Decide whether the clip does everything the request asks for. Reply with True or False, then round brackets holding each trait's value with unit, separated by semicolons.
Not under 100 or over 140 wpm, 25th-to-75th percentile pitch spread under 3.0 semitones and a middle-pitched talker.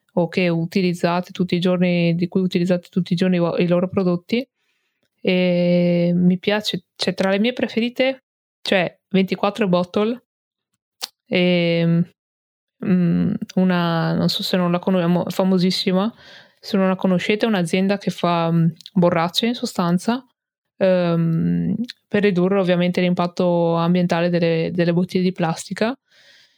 True (120 wpm; 2.4 semitones; 180 Hz)